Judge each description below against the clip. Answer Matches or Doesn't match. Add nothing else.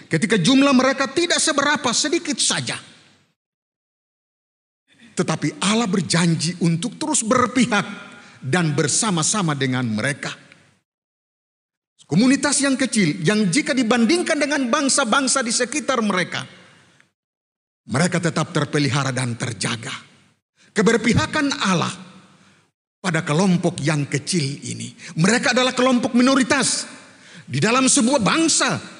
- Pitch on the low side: Doesn't match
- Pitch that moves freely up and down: Matches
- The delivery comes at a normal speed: Matches